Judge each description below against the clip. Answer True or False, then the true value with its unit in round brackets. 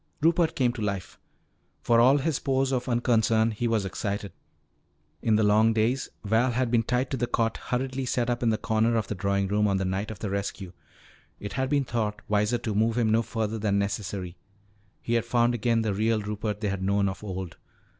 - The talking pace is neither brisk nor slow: False (215 wpm)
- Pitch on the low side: True (110 Hz)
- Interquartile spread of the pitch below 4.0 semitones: True (2.9 semitones)